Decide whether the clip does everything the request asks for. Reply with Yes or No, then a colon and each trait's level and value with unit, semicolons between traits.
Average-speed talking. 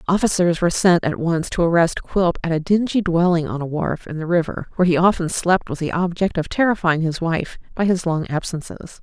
No: fast, 220 wpm